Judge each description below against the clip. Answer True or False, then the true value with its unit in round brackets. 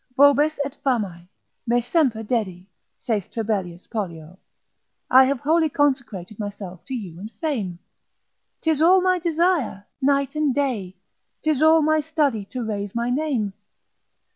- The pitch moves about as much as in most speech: False (6.7 semitones)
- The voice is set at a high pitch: True (245 Hz)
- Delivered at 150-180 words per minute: False (140 wpm)